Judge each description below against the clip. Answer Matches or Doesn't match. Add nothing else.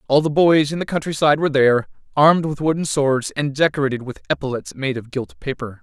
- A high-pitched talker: Doesn't match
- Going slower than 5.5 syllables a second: Doesn't match